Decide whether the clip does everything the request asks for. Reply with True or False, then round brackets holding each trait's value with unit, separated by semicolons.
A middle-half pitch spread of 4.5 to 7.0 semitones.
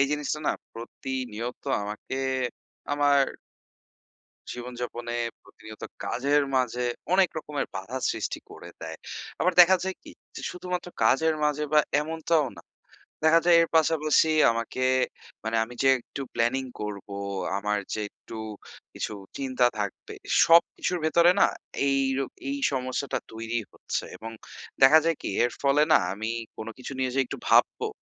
True (5.0 semitones)